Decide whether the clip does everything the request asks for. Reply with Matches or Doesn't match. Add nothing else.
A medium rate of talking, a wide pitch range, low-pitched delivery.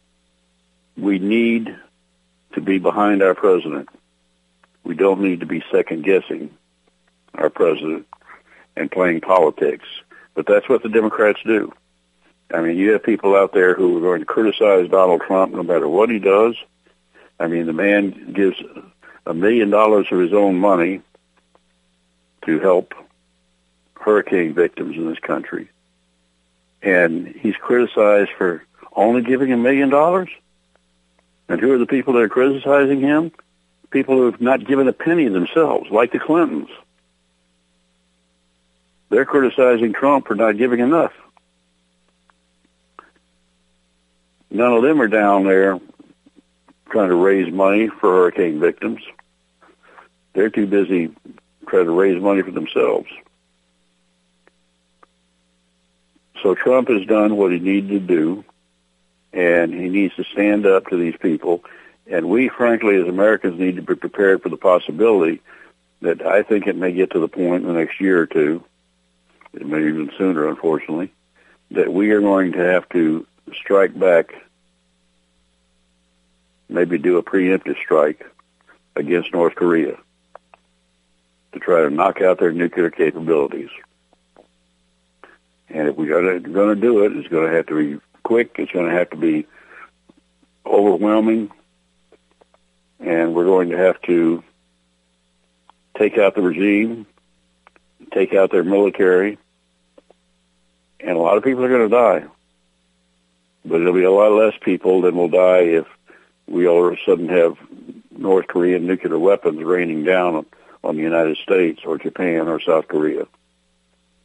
Matches